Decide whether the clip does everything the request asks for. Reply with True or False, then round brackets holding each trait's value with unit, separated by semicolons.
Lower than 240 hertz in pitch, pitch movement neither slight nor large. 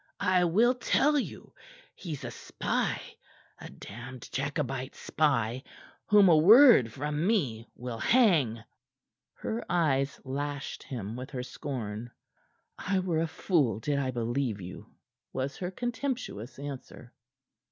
False (140 Hz; 6.7 semitones)